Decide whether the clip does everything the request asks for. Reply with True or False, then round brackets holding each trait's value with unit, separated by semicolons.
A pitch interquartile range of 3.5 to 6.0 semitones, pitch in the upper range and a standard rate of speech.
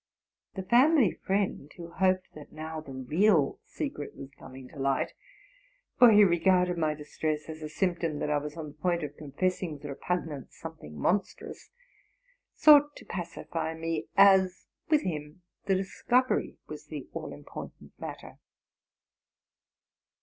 False (4.2 semitones; 165 Hz; 145 wpm)